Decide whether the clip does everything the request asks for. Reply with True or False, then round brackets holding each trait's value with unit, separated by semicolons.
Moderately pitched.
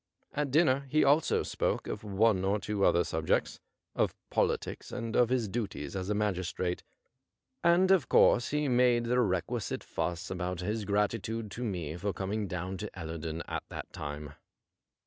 False (105 Hz)